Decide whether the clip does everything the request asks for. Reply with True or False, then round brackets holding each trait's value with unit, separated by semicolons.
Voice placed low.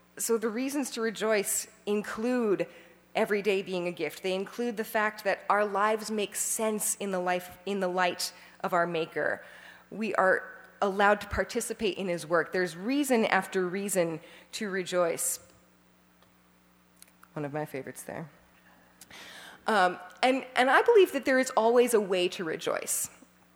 False (190 Hz)